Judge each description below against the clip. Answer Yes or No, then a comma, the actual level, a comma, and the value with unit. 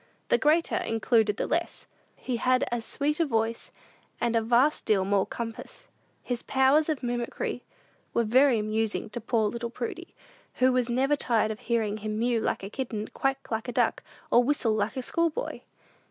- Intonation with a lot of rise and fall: No, average, 3.1 semitones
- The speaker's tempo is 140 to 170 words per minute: No, average, 180 wpm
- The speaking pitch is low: No, high, 235 Hz